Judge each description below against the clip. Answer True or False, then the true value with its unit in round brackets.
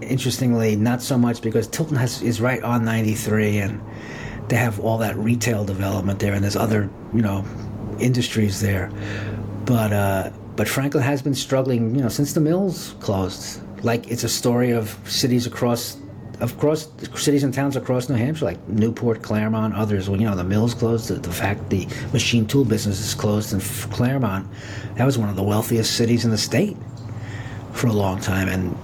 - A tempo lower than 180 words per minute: False (185 wpm)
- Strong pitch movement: False (2.7 semitones)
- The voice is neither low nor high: False (115 Hz)